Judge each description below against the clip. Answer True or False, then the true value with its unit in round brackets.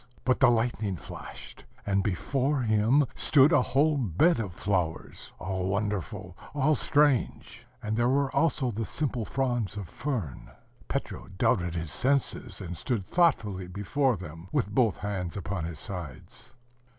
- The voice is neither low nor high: False (110 Hz)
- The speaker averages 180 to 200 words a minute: False (145 wpm)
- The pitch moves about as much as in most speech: False (6.2 semitones)